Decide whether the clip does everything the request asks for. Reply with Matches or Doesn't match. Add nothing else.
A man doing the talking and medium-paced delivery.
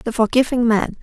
Doesn't match